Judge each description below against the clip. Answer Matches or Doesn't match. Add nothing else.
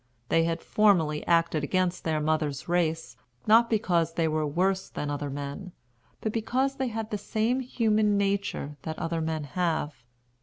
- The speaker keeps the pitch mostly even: Doesn't match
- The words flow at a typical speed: Matches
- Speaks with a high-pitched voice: Doesn't match